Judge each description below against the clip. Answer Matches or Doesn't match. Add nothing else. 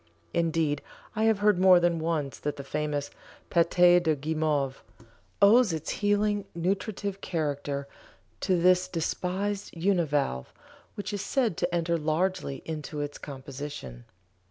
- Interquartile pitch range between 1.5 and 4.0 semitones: Doesn't match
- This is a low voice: Doesn't match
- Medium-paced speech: Doesn't match